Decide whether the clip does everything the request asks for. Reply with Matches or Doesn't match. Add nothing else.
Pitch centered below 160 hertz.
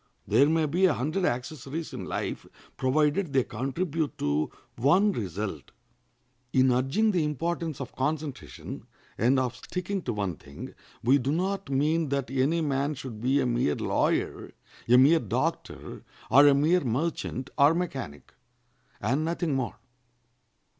Matches